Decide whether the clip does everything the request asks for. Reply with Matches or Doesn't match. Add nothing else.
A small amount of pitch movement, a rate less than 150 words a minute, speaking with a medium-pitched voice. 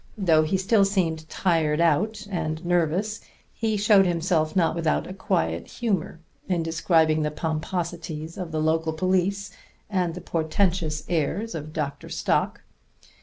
Doesn't match